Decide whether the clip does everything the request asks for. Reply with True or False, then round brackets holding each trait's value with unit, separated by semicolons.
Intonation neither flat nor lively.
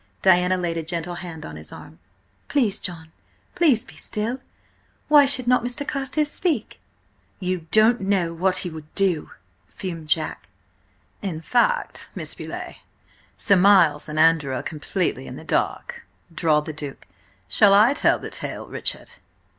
False (5.7 semitones)